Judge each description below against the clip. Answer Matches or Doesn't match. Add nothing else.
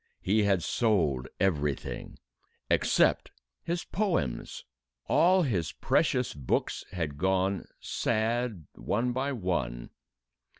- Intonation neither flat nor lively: Doesn't match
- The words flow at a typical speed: Doesn't match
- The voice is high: Doesn't match